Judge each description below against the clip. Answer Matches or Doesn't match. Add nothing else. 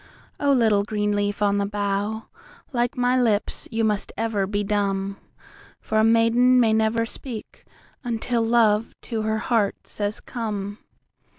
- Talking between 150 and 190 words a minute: Doesn't match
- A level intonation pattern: Matches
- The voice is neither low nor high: Doesn't match